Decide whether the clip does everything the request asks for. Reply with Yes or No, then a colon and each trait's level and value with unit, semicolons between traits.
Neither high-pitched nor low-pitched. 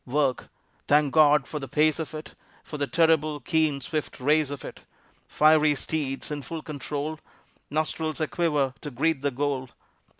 Yes: medium, 150 Hz